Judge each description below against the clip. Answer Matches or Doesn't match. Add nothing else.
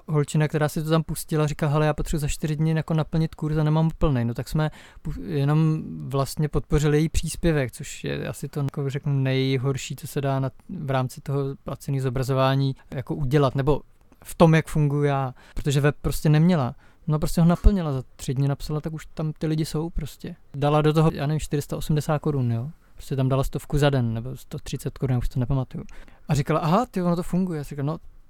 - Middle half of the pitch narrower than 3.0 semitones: Matches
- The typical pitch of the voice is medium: Matches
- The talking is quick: Matches